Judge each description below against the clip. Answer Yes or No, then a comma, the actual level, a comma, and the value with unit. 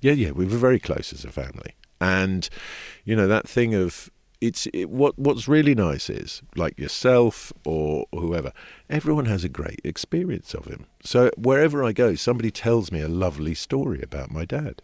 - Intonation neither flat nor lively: No, wide, 7.3 semitones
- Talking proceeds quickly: No, average, 185 wpm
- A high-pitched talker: No, low, 100 Hz